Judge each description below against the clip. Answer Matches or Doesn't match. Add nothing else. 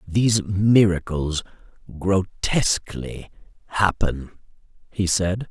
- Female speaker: Doesn't match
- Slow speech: Matches